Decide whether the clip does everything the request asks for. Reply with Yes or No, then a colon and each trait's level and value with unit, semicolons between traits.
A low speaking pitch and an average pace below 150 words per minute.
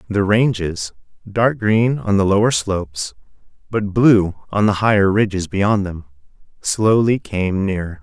Yes: low, 100 Hz; average, 140 wpm